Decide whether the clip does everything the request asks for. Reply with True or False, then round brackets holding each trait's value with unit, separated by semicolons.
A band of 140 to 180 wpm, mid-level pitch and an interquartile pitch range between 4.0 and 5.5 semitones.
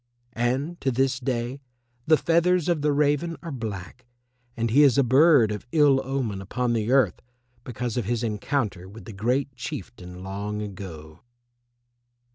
False (155 wpm; 125 Hz; 5.0 semitones)